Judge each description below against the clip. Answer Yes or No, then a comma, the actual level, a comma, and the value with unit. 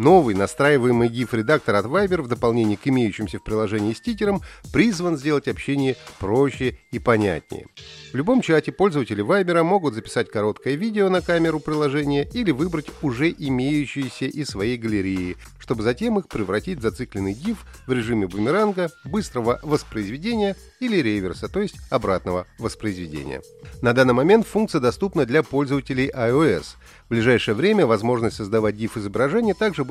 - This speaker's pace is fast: No, average, 140 wpm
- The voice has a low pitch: Yes, low, 130 Hz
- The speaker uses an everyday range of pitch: No, wide, 7.0 semitones